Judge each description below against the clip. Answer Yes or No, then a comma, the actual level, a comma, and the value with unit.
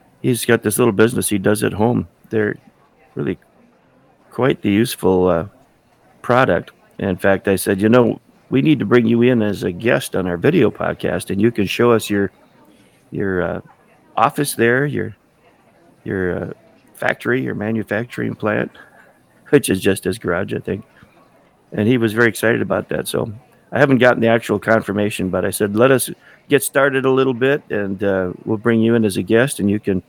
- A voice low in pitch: Yes, low, 110 Hz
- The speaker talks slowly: No, average, 190 wpm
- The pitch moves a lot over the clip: No, average, 3.3 semitones